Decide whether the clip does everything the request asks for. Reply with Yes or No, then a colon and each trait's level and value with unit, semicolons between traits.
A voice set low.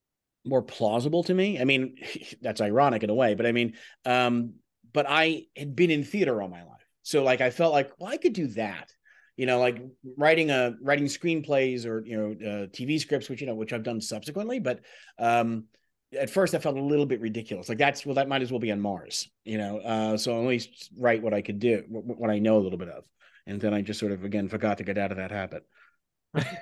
Yes: low, 125 Hz